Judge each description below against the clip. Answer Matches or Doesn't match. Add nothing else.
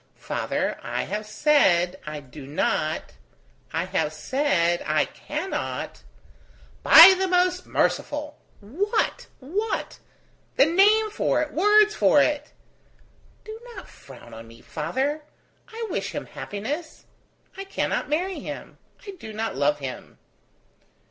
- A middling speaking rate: Doesn't match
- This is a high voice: Matches